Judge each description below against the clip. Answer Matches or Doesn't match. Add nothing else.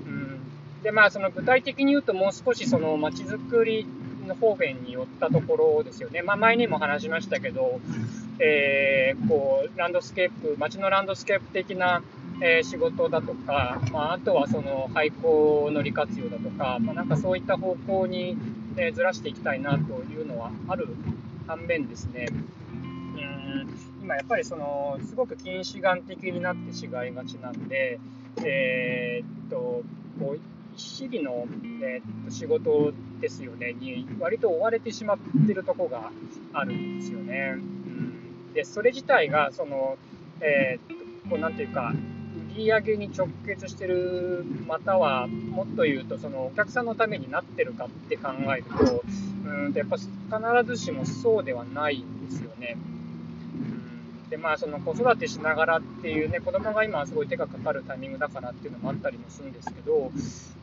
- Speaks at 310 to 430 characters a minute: Matches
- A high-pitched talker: Matches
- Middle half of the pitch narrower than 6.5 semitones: Doesn't match